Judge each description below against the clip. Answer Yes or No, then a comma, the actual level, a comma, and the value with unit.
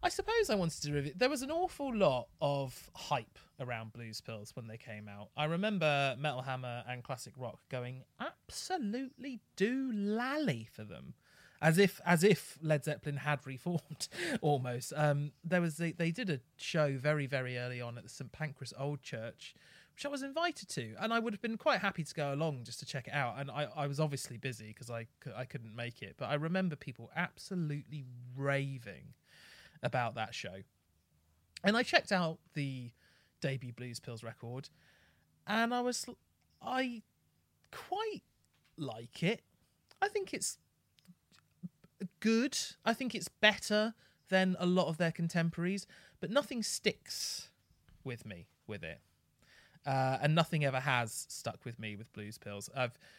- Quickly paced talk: No, average, 170 wpm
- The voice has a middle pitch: Yes, medium, 145 Hz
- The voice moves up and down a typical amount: No, wide, 7.4 semitones